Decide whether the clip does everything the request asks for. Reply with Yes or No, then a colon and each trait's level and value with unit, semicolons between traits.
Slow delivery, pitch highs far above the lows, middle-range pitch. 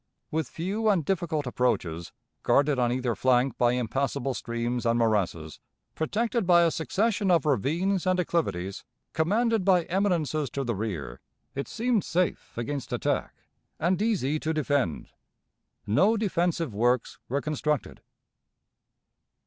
Yes: slow, 130 wpm; wide, 7.1 semitones; medium, 150 Hz